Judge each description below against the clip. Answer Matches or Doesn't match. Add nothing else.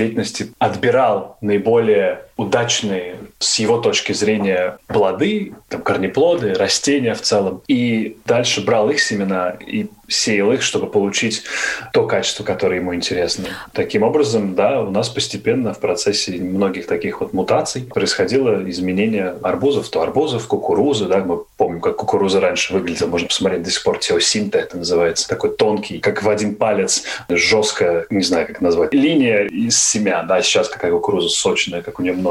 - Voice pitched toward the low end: Matches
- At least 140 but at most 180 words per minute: Matches